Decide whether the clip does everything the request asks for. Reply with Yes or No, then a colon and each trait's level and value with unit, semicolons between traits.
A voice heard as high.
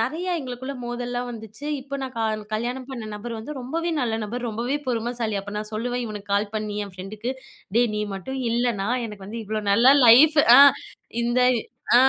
Yes: high, 235 Hz